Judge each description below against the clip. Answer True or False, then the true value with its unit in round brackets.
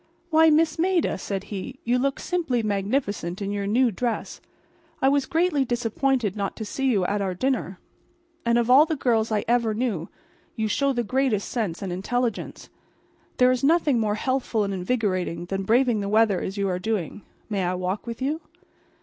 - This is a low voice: False (225 Hz)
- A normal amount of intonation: True (4.9 semitones)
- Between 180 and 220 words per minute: True (185 wpm)